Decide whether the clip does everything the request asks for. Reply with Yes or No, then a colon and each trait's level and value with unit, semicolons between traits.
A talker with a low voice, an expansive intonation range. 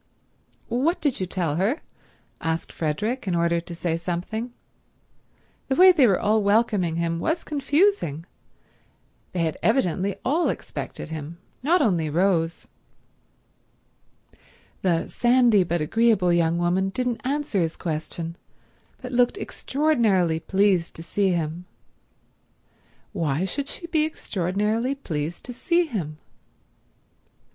No: high, 190 Hz; wide, 6.9 semitones